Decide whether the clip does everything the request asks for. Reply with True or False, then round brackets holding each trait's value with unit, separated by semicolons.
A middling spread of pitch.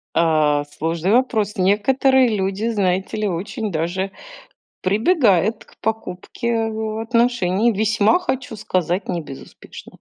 True (4.2 semitones)